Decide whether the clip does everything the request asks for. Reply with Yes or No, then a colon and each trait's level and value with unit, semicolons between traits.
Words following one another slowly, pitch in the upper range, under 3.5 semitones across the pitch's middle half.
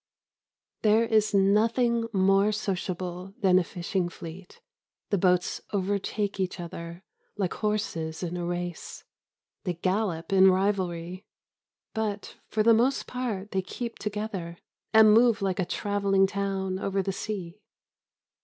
Yes: slow, 130 wpm; high, 195 Hz; average, 2.8 semitones